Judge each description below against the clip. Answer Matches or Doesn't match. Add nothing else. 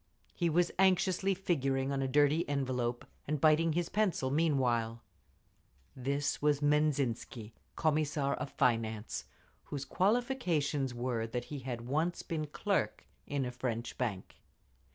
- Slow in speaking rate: Matches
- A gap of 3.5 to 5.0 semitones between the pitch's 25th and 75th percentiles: Matches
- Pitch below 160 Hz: Matches